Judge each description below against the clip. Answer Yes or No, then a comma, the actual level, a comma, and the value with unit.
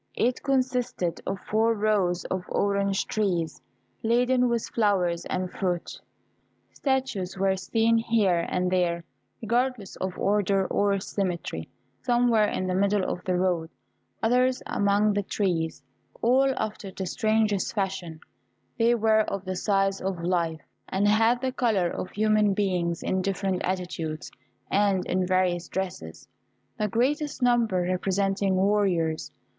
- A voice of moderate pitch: No, high, 195 Hz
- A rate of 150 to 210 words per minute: No, slow, 135 wpm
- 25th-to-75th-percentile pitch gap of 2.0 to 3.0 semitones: No, average, 3.4 semitones